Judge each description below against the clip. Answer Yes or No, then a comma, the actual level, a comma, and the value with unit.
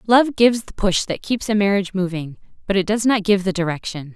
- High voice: Yes, high, 200 Hz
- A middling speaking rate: No, fast, 230 wpm